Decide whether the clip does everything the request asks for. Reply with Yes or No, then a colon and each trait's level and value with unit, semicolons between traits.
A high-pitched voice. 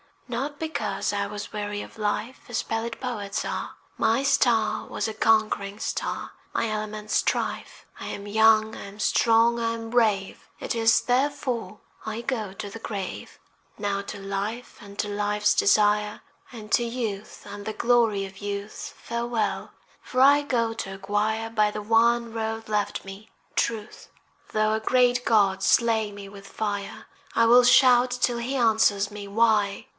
Yes: high, 220 Hz